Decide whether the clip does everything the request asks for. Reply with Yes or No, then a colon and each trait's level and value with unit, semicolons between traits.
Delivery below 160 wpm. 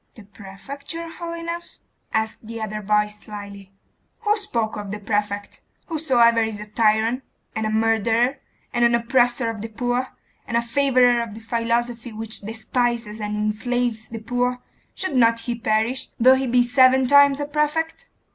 No: average, 165 wpm